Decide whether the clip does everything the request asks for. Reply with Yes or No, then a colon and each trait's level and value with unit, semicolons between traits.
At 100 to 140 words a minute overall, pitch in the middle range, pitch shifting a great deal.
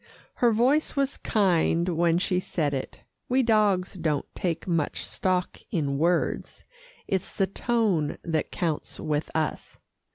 No: slow, 135 wpm; medium, 180 Hz; average, 4.8 semitones